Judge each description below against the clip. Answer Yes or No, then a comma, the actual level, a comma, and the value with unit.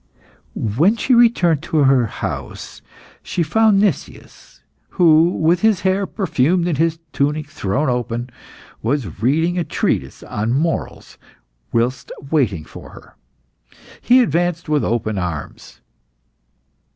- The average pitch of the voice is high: No, medium, 155 Hz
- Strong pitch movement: Yes, wide, 6.3 semitones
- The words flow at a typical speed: No, slow, 120 wpm